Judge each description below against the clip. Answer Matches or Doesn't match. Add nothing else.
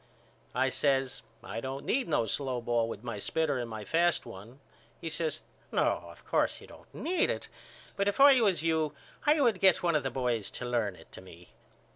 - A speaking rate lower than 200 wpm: Doesn't match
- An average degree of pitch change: Doesn't match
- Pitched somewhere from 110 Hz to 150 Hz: Matches